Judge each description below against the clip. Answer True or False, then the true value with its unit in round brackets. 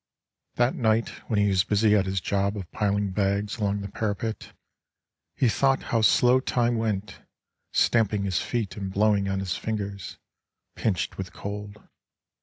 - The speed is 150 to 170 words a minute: True (155 wpm)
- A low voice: True (105 Hz)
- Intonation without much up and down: True (2.1 semitones)